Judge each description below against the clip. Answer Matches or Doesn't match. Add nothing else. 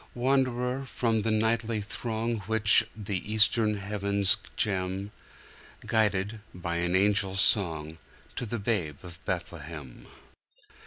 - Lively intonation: Doesn't match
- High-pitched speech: Doesn't match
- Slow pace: Matches